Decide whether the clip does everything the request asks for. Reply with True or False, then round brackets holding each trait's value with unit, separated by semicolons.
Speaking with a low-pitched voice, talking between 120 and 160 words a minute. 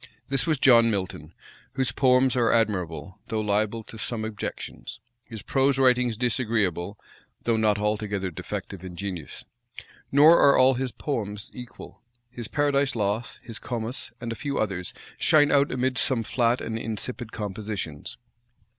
True (115 Hz; 145 wpm)